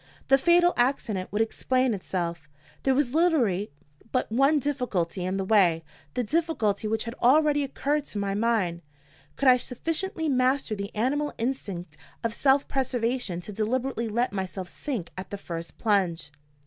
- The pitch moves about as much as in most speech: No, wide, 5.7 semitones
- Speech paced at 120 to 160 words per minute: Yes, average, 155 wpm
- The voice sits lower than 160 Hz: No, high, 230 Hz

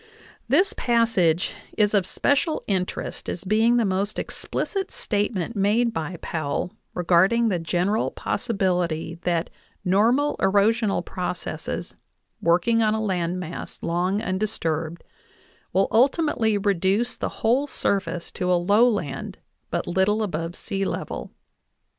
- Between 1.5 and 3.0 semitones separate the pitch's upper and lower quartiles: No, average, 4.1 semitones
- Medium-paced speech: No, slow, 115 wpm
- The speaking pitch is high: Yes, high, 195 Hz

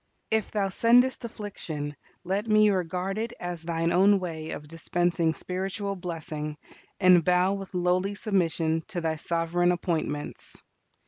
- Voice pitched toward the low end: No, medium, 180 Hz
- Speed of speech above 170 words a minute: No, slow, 135 wpm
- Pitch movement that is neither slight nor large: Yes, average, 3.1 semitones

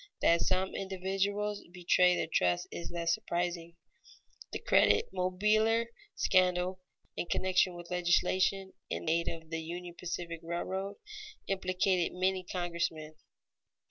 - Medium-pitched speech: Yes, medium, 180 Hz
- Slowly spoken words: Yes, slow, 115 wpm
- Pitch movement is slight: Yes, narrow, 1.8 semitones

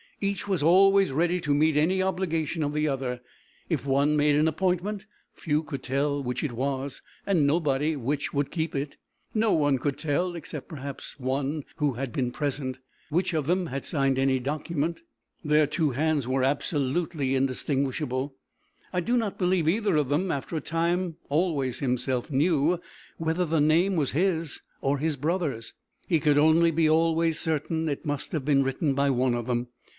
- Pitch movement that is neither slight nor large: Yes, average, 3.4 semitones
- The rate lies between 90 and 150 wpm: No, average, 175 wpm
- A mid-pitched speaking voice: Yes, medium, 150 Hz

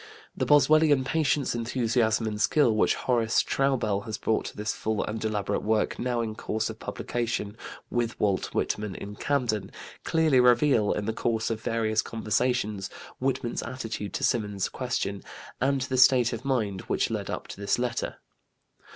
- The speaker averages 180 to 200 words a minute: No, average, 160 wpm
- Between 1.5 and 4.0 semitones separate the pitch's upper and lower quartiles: Yes, average, 3.2 semitones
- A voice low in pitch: Yes, low, 115 Hz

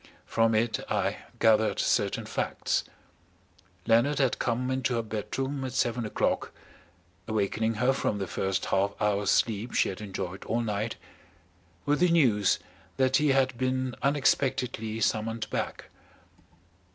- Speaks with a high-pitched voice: No, low, 115 Hz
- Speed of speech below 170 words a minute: Yes, slow, 135 wpm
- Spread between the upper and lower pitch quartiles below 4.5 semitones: Yes, average, 3.6 semitones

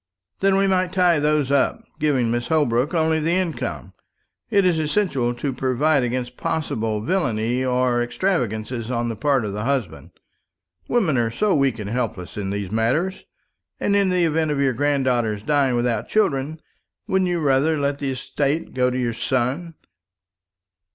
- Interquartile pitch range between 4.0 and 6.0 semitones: Yes, average, 5.0 semitones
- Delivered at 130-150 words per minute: No, average, 165 wpm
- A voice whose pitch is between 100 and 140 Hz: Yes, low, 135 Hz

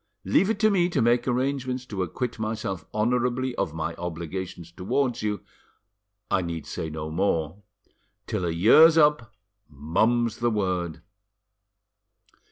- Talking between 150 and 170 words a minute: No, slow, 135 wpm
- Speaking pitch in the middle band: No, low, 105 Hz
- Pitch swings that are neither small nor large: No, wide, 6.6 semitones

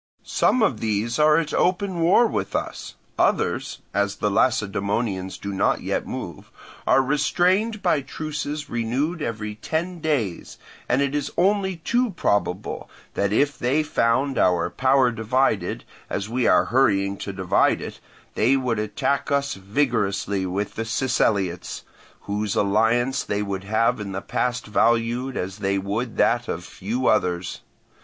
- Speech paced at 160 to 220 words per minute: No, average, 150 wpm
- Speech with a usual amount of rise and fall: No, wide, 6.0 semitones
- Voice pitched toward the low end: Yes, low, 115 Hz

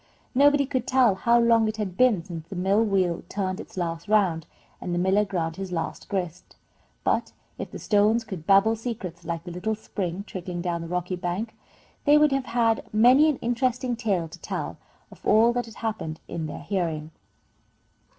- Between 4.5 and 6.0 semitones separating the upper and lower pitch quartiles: Yes, average, 4.8 semitones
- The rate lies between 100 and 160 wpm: No, average, 190 wpm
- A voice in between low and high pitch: No, high, 200 Hz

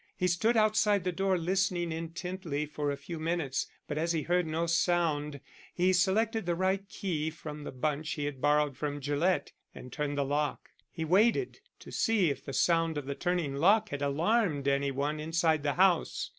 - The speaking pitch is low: No, medium, 165 Hz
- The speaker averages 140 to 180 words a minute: No, average, 190 wpm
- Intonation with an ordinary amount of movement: Yes, average, 4.0 semitones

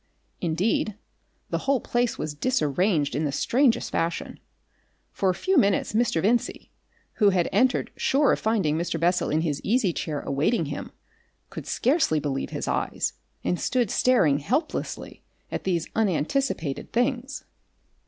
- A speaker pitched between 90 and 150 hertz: No, high, 190 Hz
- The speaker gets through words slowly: No, average, 145 wpm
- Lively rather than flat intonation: Yes, wide, 7.6 semitones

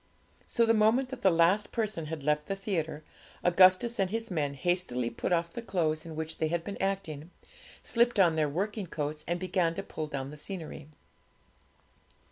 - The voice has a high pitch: No, medium, 175 Hz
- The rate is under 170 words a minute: No, average, 185 wpm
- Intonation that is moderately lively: Yes, average, 4.2 semitones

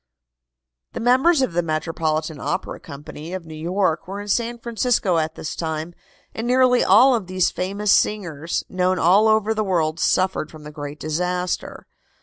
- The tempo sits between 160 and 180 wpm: Yes, average, 165 wpm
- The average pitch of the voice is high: No, medium, 180 Hz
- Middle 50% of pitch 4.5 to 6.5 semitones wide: Yes, average, 5.2 semitones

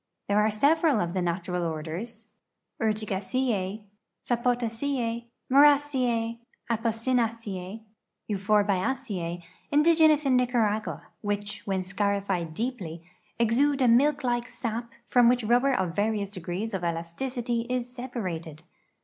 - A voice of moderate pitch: No, high, 225 Hz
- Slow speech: Yes, slow, 115 wpm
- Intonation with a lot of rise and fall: No, average, 4.5 semitones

